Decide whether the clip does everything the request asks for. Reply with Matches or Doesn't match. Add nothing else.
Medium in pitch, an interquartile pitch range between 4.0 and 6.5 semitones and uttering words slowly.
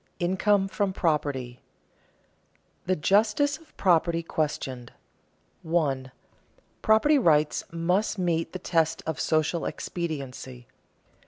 Matches